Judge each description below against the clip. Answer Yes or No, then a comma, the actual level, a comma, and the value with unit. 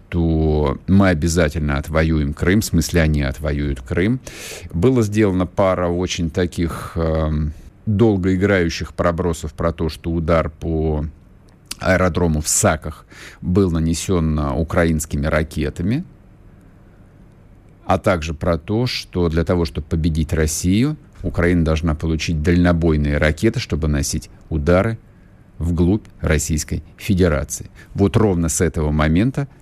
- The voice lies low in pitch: Yes, very low, 85 Hz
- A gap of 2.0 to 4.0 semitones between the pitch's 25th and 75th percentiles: Yes, average, 3.4 semitones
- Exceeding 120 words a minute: No, average, 115 wpm